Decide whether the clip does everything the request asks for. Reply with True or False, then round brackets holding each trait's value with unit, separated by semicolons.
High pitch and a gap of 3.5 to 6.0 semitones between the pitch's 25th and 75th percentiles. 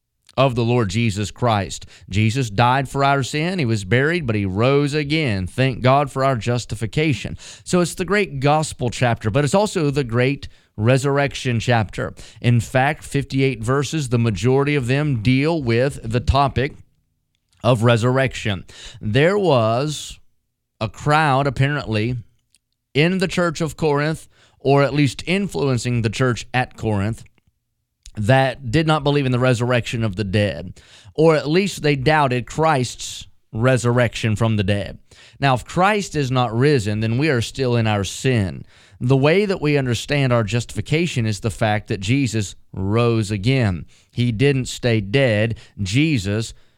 False (125 Hz; 4.2 semitones)